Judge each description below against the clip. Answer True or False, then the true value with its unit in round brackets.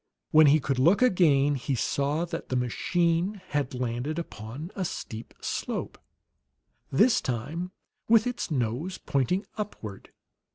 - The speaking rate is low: True (130 wpm)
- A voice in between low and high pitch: True (150 Hz)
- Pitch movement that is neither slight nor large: False (5.8 semitones)